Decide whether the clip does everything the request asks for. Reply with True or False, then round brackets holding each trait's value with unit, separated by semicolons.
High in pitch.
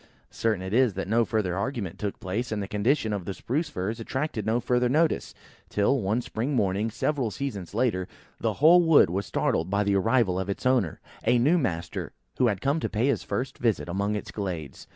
False (110 Hz)